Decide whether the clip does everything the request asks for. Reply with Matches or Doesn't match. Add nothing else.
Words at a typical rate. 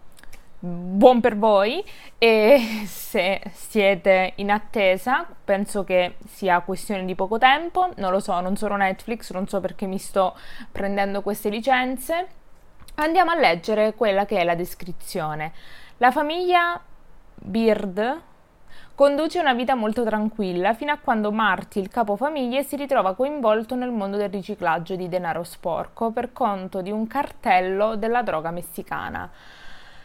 Matches